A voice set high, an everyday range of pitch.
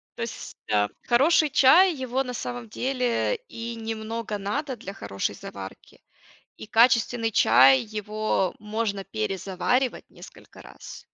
Yes: high, 225 Hz; average, 4.5 semitones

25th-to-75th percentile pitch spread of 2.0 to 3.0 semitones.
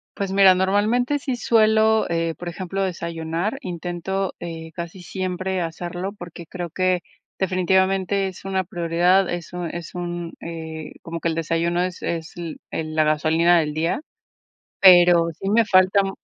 Yes: narrow, 2.4 semitones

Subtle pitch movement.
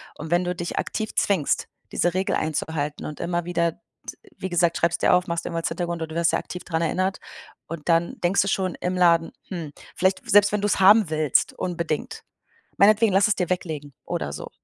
Yes: narrow, 2.3 semitones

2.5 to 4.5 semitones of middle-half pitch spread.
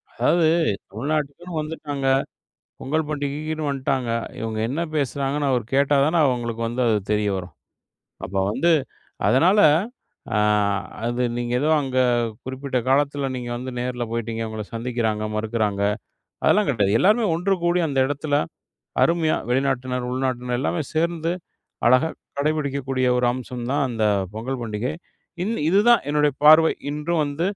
Yes: average, 4.1 semitones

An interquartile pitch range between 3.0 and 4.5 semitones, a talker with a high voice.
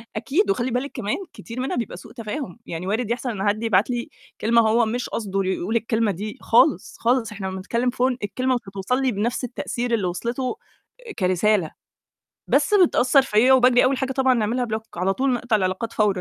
Yes: average, 3.6 semitones; high, 230 Hz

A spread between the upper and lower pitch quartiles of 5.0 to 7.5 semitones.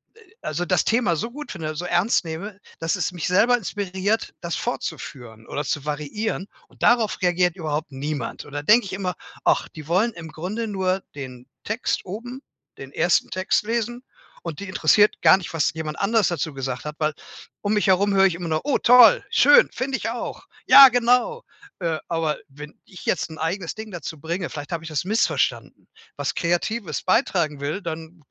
Yes: wide, 5.4 semitones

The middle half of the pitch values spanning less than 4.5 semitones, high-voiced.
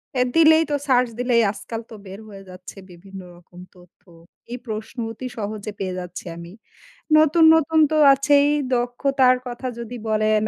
No: average, 5.1 semitones; high, 235 Hz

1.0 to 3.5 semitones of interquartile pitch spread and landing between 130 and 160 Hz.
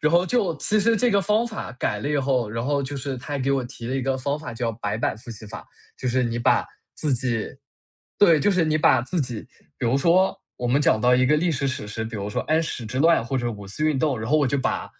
No: average, 4.6 semitones; low, 135 Hz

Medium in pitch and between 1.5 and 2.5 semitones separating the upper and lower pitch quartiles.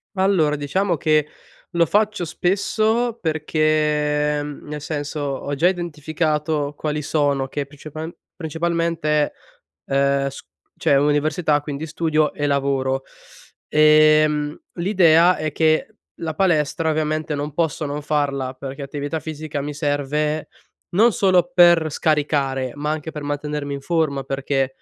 Yes: medium, 150 Hz; narrow, 2.0 semitones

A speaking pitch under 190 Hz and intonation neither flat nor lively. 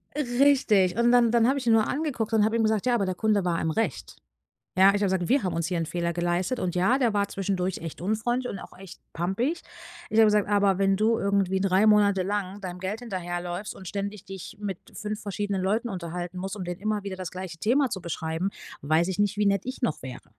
No: high, 200 Hz; average, 3.3 semitones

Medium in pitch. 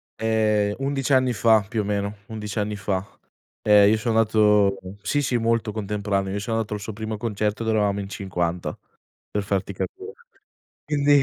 No: low, 105 Hz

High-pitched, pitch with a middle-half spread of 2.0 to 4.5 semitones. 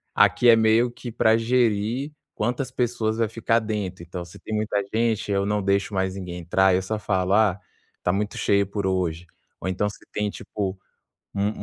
No: low, 105 Hz; average, 2.8 semitones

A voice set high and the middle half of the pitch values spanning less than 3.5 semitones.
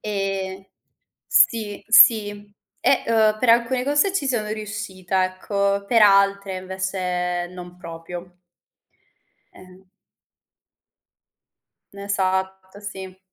Yes: high, 200 Hz; narrow, 2.4 semitones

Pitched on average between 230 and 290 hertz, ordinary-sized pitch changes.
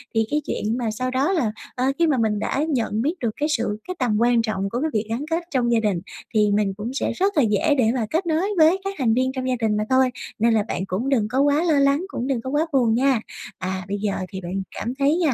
Yes: very high, 250 Hz; average, 4.8 semitones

